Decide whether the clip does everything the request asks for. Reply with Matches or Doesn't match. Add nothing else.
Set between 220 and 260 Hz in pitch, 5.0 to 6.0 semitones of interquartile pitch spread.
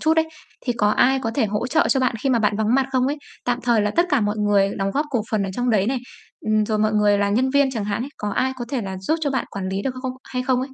Doesn't match